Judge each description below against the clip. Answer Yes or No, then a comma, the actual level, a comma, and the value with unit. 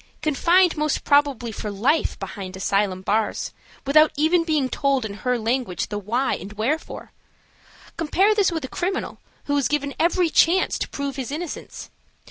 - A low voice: No, very high, 280 Hz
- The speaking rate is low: No, average, 160 wpm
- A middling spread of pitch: No, wide, 6.5 semitones